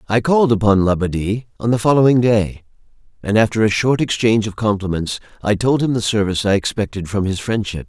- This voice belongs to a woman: No, male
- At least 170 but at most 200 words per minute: Yes, average, 190 wpm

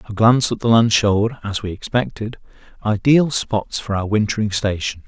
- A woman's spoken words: No, male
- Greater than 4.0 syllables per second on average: Yes, 5.2 syllables/s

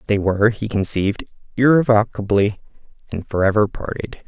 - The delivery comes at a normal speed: No, slow, 125 wpm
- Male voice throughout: Yes, male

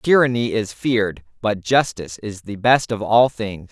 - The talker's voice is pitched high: No, low, 110 Hz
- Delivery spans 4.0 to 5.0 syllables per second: Yes, 4.6 syllables/s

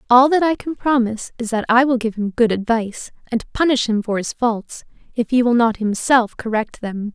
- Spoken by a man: No, female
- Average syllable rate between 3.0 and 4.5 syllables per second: No, 5.2 syllables/s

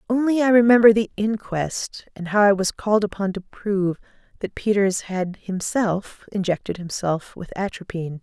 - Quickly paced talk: No, average, 155 wpm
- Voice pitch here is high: Yes, high, 200 Hz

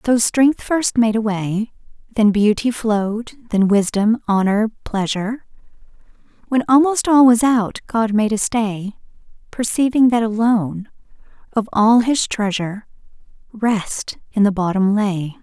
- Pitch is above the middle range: Yes, high, 220 Hz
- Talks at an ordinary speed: No, slow, 130 wpm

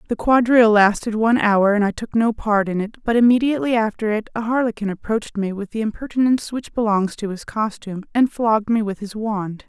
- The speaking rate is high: Yes, fast, 210 wpm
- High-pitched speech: Yes, high, 220 Hz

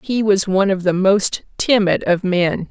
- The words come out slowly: No, average, 200 wpm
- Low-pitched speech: No, high, 195 Hz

